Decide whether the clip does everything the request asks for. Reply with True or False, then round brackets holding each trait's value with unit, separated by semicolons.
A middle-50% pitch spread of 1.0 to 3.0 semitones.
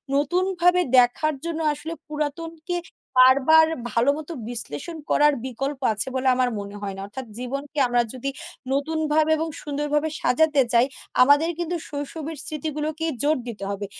False (3.7 semitones)